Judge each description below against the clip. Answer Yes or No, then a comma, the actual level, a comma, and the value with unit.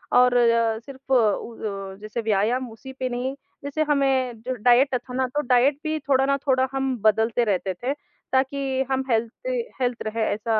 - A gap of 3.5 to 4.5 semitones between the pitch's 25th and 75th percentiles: No, average, 3.0 semitones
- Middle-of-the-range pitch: No, very high, 250 Hz